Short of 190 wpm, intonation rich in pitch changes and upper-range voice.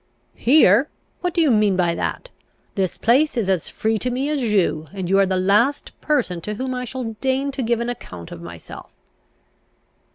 No: average, 195 wpm; wide, 5.8 semitones; high, 225 Hz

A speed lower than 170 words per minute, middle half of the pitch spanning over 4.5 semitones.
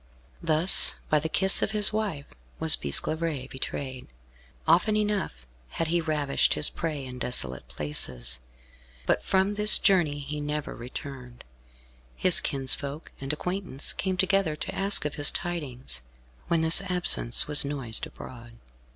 Yes: average, 140 wpm; wide, 5.4 semitones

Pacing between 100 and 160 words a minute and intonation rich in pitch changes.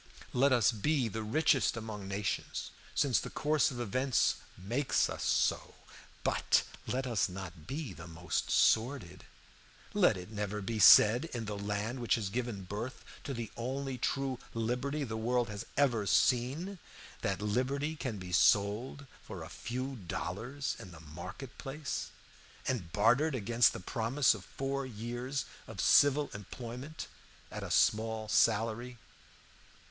No: average, 145 wpm; average, 4.4 semitones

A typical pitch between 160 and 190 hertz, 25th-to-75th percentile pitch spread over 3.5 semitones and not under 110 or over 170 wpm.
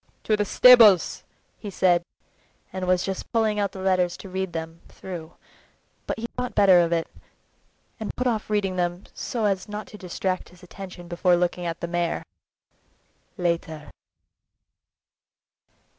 No: medium, 185 Hz; average, 3.0 semitones; average, 150 wpm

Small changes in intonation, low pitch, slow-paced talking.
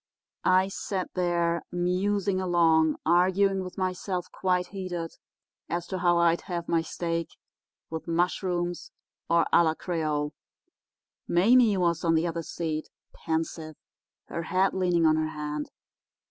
No: narrow, 2.0 semitones; medium, 175 Hz; slow, 130 wpm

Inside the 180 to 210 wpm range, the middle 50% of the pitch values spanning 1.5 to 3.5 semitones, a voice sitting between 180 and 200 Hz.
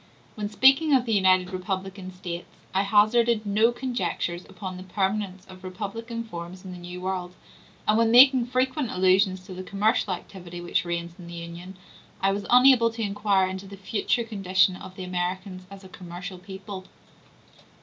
No: average, 170 wpm; average, 2.9 semitones; high, 190 Hz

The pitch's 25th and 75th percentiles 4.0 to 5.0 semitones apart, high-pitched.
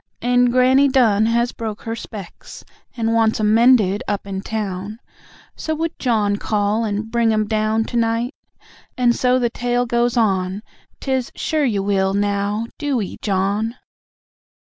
No: average, 3.0 semitones; high, 225 Hz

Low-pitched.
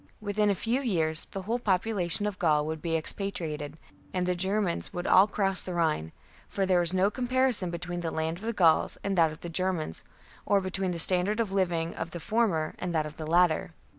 No: medium, 180 Hz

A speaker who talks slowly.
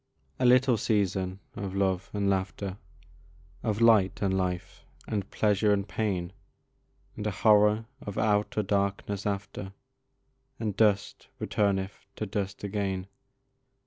Yes: slow, 120 wpm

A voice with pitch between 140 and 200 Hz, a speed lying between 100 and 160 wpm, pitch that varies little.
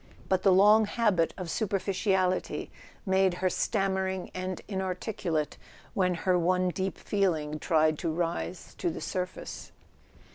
Yes: medium, 185 Hz; slow, 135 wpm; narrow, 1.7 semitones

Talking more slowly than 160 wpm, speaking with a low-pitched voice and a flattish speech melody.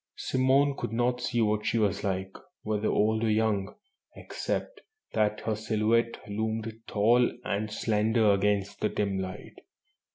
Yes: average, 140 wpm; low, 110 Hz; narrow, 1.8 semitones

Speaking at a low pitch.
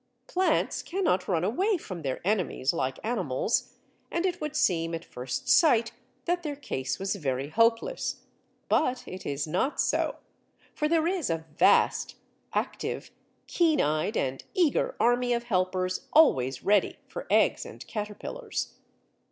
No: high, 215 Hz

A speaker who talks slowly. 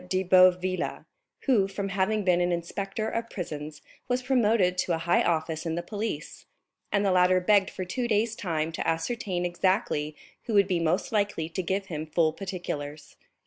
No: average, 180 wpm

